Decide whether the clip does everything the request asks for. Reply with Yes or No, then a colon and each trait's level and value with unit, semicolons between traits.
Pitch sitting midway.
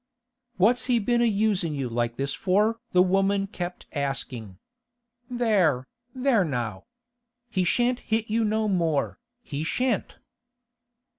No: high, 195 Hz